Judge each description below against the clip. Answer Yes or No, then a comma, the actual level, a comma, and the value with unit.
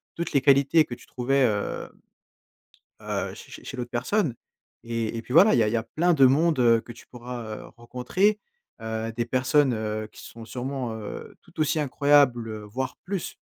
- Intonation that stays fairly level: No, average, 3.9 semitones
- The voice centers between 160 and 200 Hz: No, low, 125 Hz